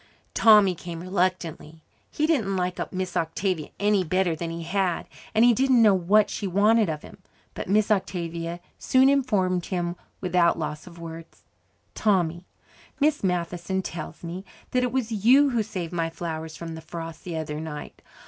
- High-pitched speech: No, medium, 180 Hz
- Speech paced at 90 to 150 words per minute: No, average, 165 wpm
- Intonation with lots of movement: No, average, 3.9 semitones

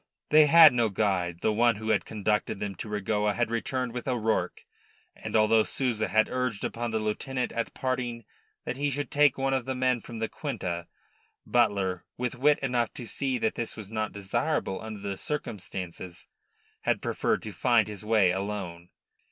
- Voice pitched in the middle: No, low, 110 Hz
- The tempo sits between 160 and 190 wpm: Yes, average, 180 wpm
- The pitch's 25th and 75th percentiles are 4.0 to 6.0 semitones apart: No, average, 3.6 semitones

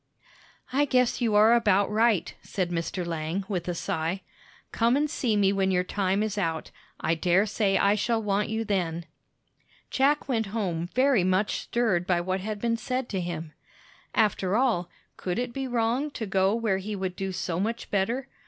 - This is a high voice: Yes, high, 200 Hz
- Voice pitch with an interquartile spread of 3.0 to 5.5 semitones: Yes, average, 4.0 semitones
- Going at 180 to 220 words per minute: Yes, average, 185 wpm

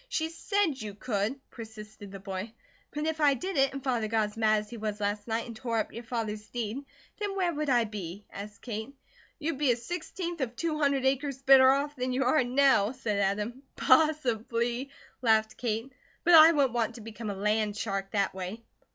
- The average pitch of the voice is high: Yes, high, 235 Hz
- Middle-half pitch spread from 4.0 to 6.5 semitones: Yes, average, 4.5 semitones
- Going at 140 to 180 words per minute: No, fast, 205 wpm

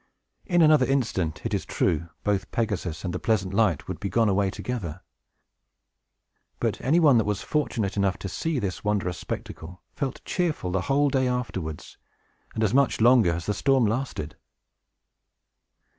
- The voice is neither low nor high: No, low, 105 Hz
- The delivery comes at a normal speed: Yes, average, 160 wpm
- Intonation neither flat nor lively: No, wide, 5.9 semitones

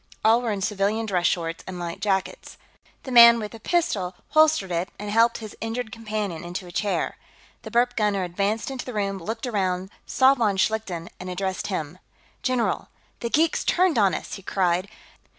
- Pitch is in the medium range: No, high, 210 Hz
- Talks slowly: No, average, 185 wpm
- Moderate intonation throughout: Yes, average, 3.9 semitones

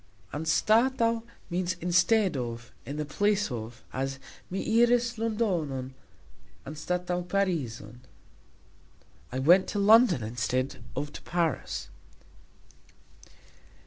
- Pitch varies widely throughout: Yes, wide, 7.9 semitones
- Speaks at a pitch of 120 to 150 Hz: No, medium, 175 Hz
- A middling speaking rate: No, slow, 95 wpm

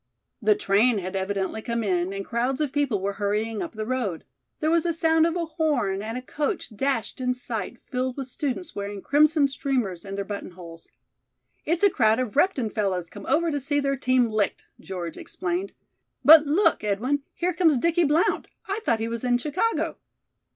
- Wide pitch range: Yes, wide, 6.7 semitones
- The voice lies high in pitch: Yes, very high, 250 Hz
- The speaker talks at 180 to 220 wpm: Yes, average, 190 wpm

